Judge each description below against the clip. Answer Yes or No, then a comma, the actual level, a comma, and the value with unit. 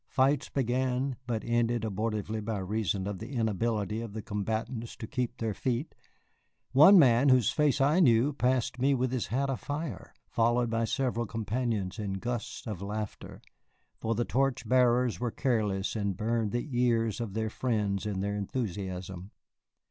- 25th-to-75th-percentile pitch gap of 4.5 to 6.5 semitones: No, average, 3.1 semitones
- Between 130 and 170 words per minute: Yes, average, 160 wpm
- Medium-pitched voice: No, low, 115 Hz